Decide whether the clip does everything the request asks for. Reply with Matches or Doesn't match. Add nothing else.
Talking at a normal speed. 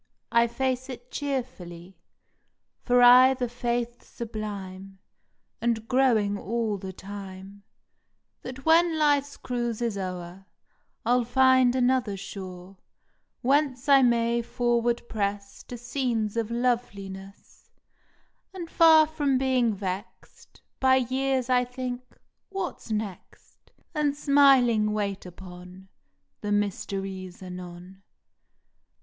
Doesn't match